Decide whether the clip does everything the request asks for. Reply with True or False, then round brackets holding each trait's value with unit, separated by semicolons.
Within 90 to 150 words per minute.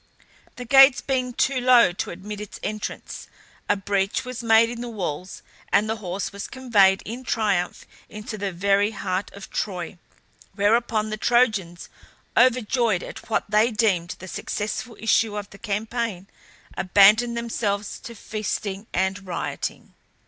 True (145 wpm)